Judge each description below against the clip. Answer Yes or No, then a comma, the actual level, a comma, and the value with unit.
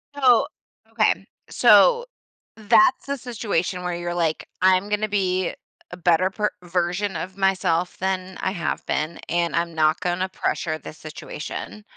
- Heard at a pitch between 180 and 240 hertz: Yes, medium, 185 Hz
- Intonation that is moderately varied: Yes, average, 3.2 semitones